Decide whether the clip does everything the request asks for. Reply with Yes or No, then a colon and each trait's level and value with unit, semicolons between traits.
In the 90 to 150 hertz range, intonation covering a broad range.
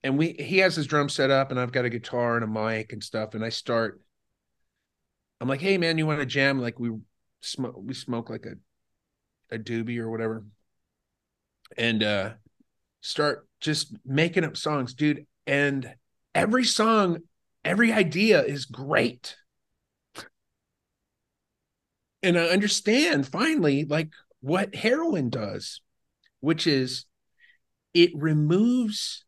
Yes: medium, 140 Hz; wide, 6.7 semitones